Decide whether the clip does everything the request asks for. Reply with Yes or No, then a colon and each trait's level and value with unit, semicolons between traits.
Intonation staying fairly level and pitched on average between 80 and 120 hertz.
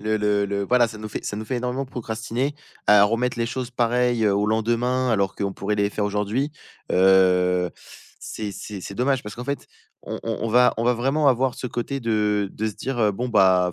No: average, 3.3 semitones; low, 110 Hz